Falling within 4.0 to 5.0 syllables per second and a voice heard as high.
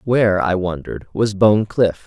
No: 4.8 syllables/s; low, 100 Hz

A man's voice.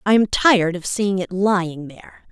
No: female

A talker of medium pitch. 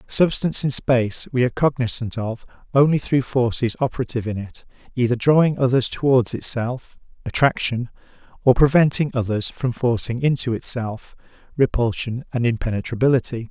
No: low, 125 Hz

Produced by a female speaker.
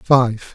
No: male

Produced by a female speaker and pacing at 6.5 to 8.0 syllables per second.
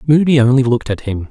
No: male; 6.8 syllables/s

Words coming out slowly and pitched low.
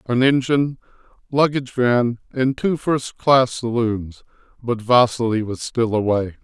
Yes: slow, 120 wpm; low, 120 Hz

